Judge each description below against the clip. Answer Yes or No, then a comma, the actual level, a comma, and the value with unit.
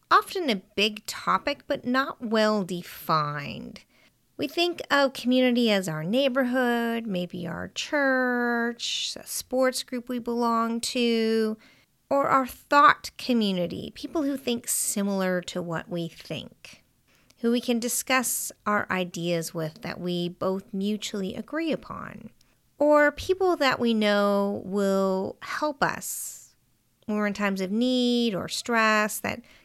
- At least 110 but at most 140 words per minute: Yes, slow, 135 wpm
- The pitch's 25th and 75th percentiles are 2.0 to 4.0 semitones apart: No, average, 4.8 semitones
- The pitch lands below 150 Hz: No, high, 230 Hz